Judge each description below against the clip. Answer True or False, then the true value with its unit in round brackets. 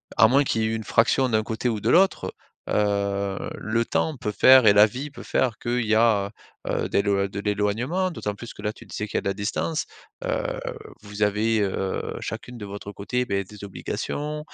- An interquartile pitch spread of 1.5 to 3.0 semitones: False (3.5 semitones)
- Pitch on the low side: True (110 Hz)